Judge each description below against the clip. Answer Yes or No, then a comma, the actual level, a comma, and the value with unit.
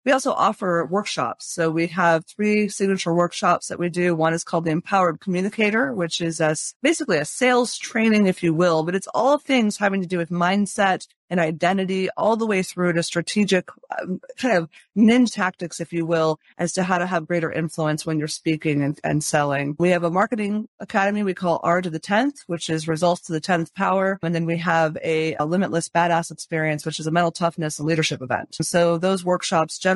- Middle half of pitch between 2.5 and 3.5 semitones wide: Yes, average, 3.1 semitones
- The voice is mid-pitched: Yes, medium, 175 Hz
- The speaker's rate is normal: No, fast, 210 wpm